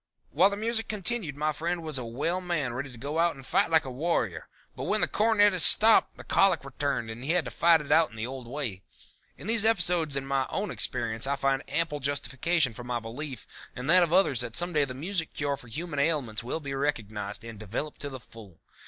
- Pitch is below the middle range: No, medium, 145 Hz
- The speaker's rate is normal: No, fast, 230 wpm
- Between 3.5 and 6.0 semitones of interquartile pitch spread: Yes, wide, 5.6 semitones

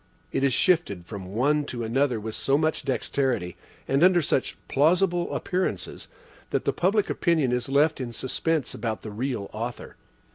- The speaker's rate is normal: Yes, average, 160 wpm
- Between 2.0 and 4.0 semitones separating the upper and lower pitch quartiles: No, wide, 5.5 semitones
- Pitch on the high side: No, low, 135 Hz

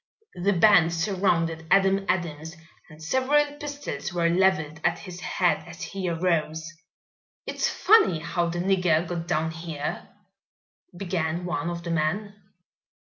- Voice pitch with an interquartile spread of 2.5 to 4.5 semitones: Yes, average, 2.9 semitones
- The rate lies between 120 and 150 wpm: Yes, average, 140 wpm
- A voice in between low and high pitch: Yes, medium, 175 Hz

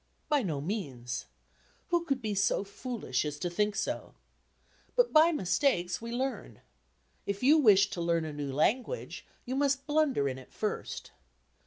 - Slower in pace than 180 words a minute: Yes, average, 160 wpm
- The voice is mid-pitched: No, high, 210 Hz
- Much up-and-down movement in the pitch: Yes, wide, 8.7 semitones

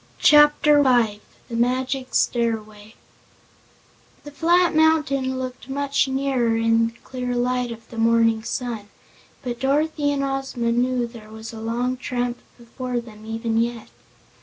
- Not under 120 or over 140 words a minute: Yes, slow, 135 wpm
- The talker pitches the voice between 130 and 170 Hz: No, high, 245 Hz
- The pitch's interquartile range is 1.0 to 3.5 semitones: Yes, average, 2.8 semitones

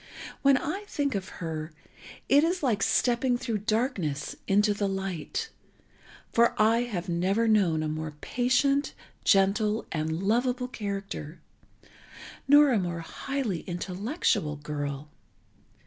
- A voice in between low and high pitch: No, high, 205 Hz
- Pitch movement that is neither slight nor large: No, wide, 6.4 semitones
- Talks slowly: Yes, slow, 120 wpm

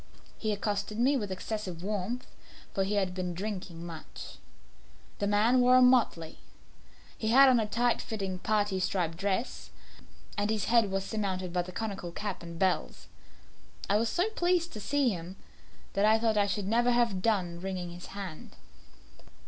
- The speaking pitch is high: Yes, high, 205 Hz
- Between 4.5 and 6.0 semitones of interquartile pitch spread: No, average, 3.7 semitones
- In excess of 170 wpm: No, average, 165 wpm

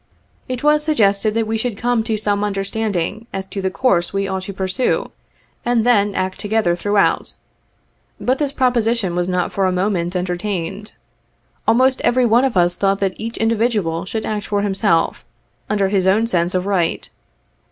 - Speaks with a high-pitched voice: Yes, high, 205 Hz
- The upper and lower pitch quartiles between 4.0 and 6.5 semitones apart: No, average, 3.4 semitones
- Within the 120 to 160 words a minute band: No, average, 180 wpm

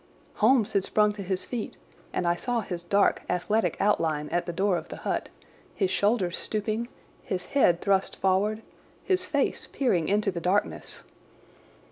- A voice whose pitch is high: Yes, high, 200 Hz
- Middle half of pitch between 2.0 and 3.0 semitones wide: No, average, 3.4 semitones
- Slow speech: No, average, 160 wpm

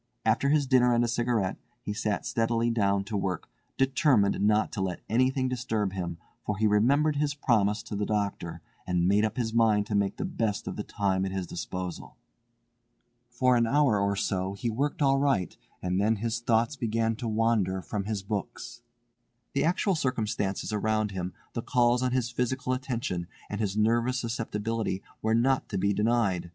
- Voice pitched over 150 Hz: No, low, 110 Hz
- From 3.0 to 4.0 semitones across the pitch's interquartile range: Yes, average, 3.5 semitones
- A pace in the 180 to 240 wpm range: Yes, average, 185 wpm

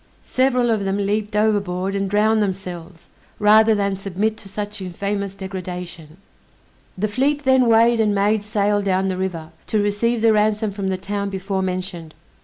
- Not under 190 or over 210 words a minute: No, average, 165 wpm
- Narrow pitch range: Yes, narrow, 2.2 semitones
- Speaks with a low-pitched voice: No, high, 200 Hz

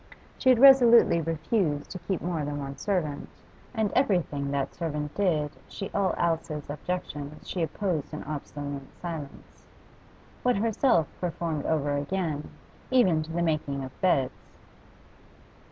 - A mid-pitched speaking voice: Yes, medium, 160 Hz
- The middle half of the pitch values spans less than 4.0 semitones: No, average, 4.5 semitones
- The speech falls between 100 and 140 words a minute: Yes, slow, 135 wpm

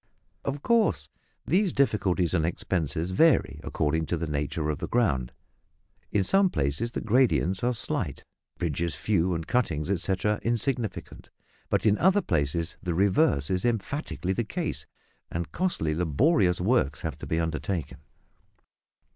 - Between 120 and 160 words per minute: Yes, average, 140 wpm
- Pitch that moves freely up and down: Yes, wide, 7.0 semitones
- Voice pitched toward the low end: Yes, very low, 95 Hz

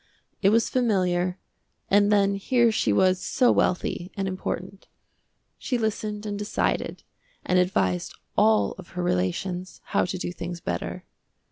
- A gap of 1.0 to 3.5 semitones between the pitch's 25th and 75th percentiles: Yes, average, 2.7 semitones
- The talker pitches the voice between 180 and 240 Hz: Yes, medium, 185 Hz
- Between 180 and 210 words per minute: No, average, 140 wpm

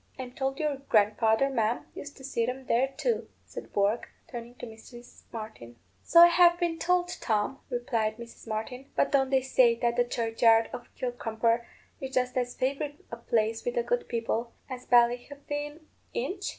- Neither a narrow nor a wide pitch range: Yes, average, 3.3 semitones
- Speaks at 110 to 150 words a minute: No, average, 175 wpm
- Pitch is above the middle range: Yes, high, 245 Hz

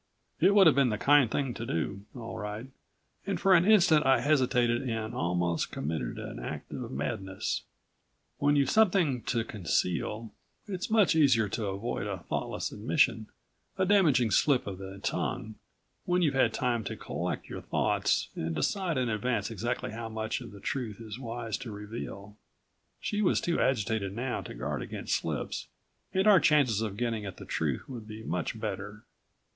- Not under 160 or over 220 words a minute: Yes, average, 175 wpm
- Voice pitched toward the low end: Yes, low, 115 Hz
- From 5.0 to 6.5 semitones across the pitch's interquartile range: Yes, wide, 5.4 semitones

